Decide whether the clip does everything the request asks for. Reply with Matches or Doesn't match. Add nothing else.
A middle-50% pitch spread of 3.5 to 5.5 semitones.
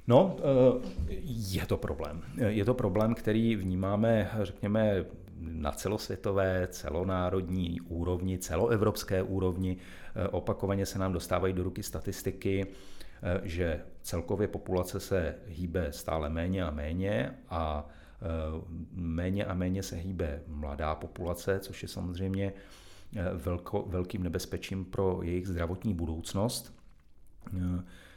Doesn't match